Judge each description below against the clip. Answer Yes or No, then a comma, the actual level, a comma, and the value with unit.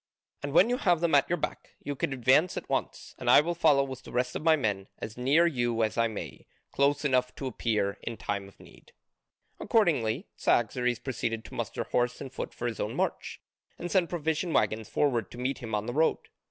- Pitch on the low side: Yes, low, 130 Hz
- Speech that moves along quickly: Yes, fast, 220 wpm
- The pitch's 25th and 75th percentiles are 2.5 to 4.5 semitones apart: No, average, 5.2 semitones